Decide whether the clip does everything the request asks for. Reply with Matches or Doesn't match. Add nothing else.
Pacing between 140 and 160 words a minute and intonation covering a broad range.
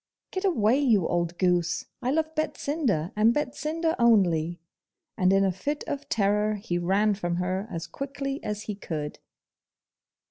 Matches